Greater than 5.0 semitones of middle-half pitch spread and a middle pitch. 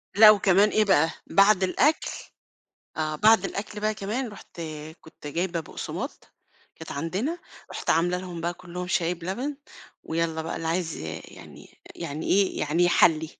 No: average, 4.0 semitones; medium, 180 Hz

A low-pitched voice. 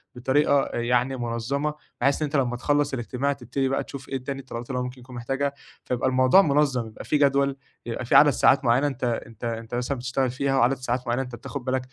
Yes: low, 130 Hz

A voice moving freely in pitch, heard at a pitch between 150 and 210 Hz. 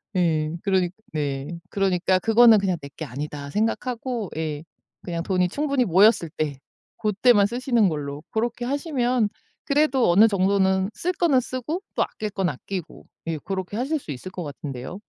Yes: wide, 6.6 semitones; high, 195 Hz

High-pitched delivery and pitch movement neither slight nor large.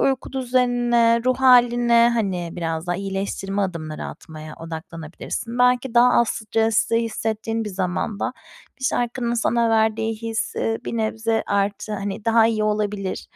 Yes: high, 225 Hz; average, 3.3 semitones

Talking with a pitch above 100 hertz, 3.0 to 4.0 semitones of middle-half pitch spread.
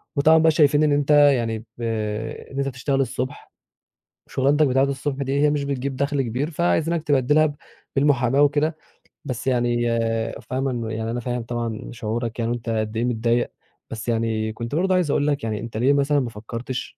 Yes: low, 135 Hz; average, 3.7 semitones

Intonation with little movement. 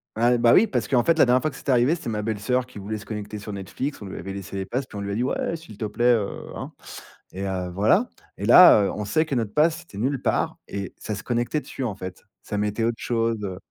No: average, 4.0 semitones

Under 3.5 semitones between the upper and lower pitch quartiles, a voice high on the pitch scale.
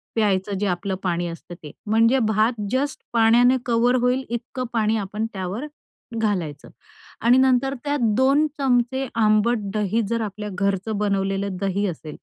No: average, 3.9 semitones; high, 215 Hz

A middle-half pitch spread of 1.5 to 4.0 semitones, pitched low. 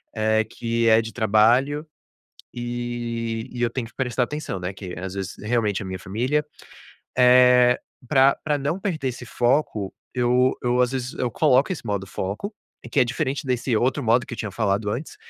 Yes: average, 2.8 semitones; low, 120 Hz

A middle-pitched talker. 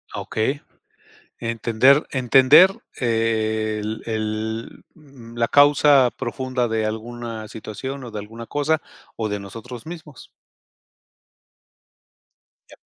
No: low, 115 Hz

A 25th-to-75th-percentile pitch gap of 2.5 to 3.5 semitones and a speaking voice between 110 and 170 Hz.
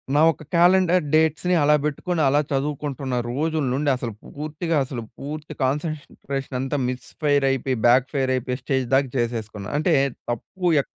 Yes: average, 3.1 semitones; medium, 140 Hz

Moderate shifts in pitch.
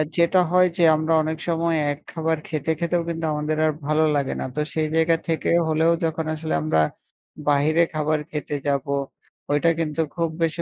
No: narrow, 1.5 semitones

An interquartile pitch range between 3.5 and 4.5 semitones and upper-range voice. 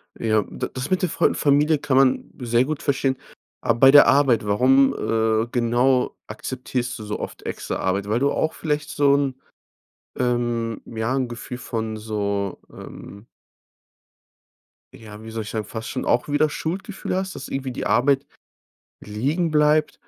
No: average, 4.1 semitones; low, 125 Hz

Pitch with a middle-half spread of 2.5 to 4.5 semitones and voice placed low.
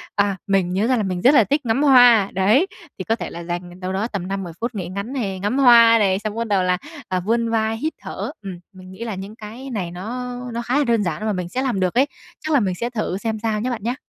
No: average, 4.1 semitones; high, 215 Hz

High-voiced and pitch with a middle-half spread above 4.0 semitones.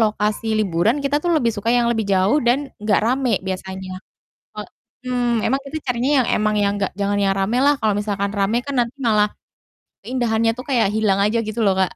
No: high, 220 Hz; average, 3.5 semitones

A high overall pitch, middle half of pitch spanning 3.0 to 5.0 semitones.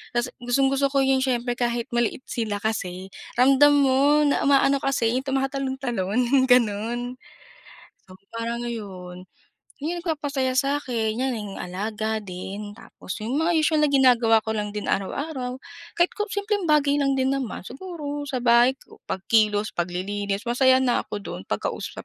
Yes: very high, 250 Hz; average, 4.3 semitones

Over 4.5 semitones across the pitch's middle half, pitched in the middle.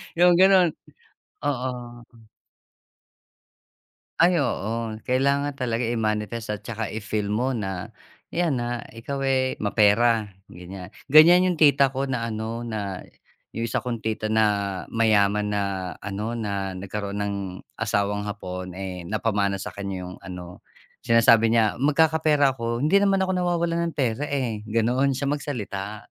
No: average, 5.2 semitones; low, 115 Hz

